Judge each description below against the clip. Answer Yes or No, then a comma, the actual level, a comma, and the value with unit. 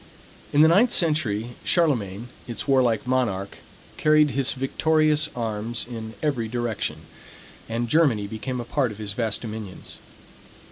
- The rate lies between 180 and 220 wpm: No, slow, 135 wpm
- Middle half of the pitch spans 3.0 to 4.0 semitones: No, average, 5.1 semitones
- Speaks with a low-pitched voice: Yes, low, 120 Hz